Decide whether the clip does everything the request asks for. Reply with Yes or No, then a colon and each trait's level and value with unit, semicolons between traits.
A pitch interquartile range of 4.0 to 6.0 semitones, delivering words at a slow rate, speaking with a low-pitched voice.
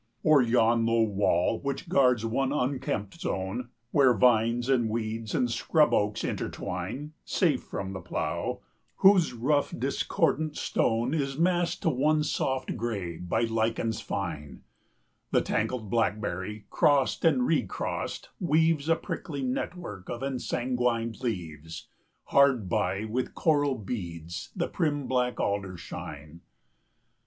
Yes: average, 5.2 semitones; slow, 130 wpm; low, 120 Hz